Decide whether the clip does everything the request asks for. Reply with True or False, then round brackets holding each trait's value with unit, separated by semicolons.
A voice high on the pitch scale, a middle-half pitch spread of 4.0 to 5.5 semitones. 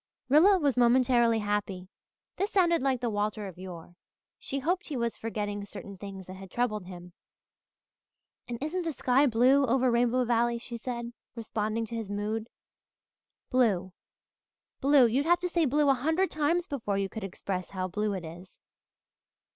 True (235 Hz; 5.1 semitones)